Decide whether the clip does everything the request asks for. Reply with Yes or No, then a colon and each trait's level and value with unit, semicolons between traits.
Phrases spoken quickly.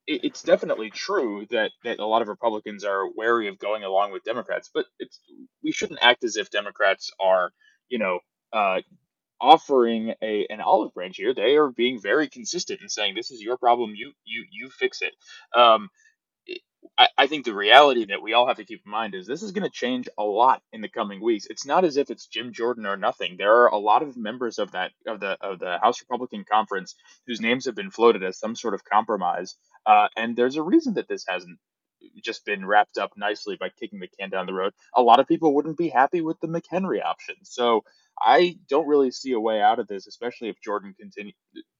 Yes: fast, 220 wpm